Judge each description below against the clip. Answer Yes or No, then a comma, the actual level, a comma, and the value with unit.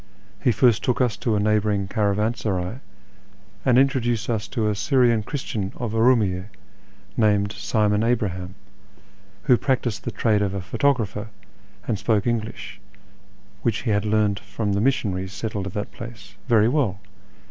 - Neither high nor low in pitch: No, low, 105 Hz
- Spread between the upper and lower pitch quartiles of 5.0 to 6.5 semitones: No, average, 2.8 semitones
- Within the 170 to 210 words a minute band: No, average, 145 wpm